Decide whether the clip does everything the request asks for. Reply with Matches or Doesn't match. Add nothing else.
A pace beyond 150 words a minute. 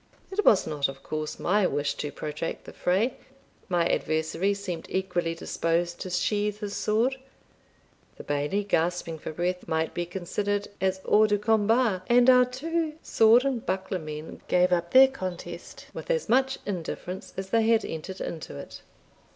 Matches